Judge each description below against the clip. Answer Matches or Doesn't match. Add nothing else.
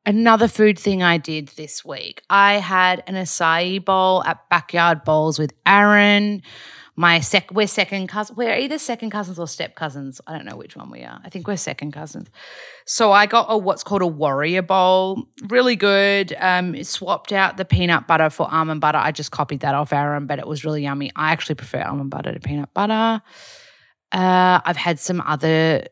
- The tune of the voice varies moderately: Matches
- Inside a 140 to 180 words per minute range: Doesn't match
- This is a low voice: Doesn't match